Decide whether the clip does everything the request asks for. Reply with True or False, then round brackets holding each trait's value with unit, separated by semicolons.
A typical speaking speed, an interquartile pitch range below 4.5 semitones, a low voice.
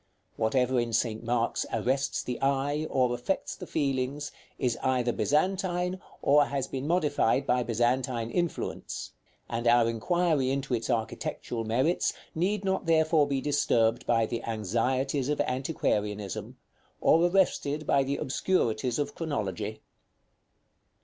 False (130 wpm; 4.1 semitones; 130 Hz)